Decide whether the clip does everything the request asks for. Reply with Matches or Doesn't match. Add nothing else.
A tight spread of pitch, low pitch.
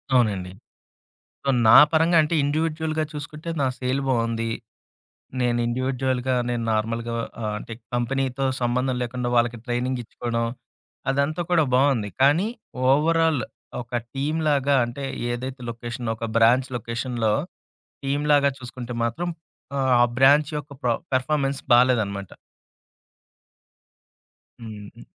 Doesn't match